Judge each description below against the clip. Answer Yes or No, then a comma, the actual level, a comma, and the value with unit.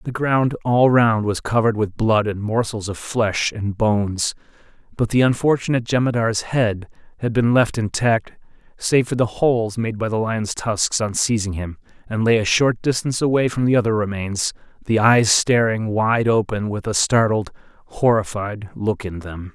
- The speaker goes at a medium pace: Yes, average, 175 wpm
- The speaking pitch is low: Yes, low, 110 Hz